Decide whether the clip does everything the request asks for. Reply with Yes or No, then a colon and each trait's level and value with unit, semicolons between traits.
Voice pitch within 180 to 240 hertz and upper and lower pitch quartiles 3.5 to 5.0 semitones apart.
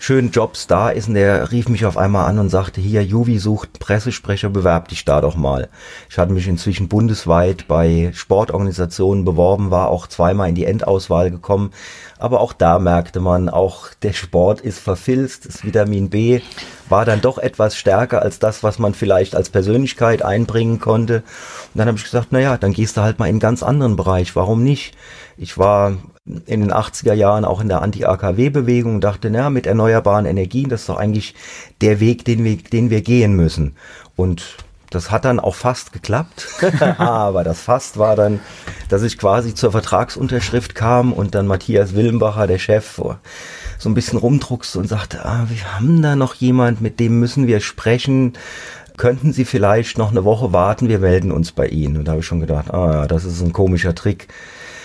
No: low, 105 Hz; average, 4.2 semitones